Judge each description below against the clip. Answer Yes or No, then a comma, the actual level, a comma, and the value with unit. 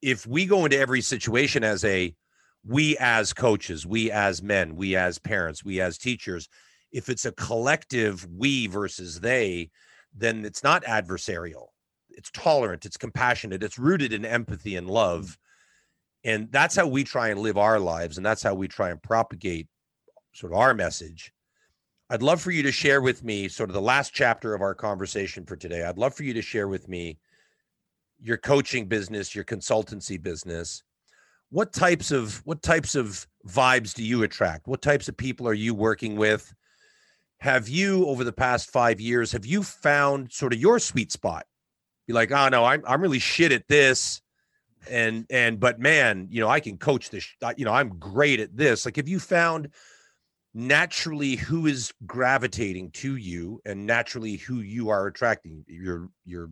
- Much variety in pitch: No, average, 5.0 semitones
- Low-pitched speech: Yes, low, 115 Hz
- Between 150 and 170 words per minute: No, average, 180 wpm